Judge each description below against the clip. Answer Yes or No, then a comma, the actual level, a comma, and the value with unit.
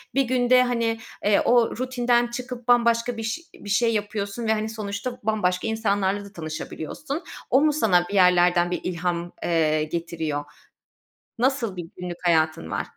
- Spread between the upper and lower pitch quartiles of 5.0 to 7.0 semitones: Yes, average, 5.3 semitones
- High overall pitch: Yes, high, 210 Hz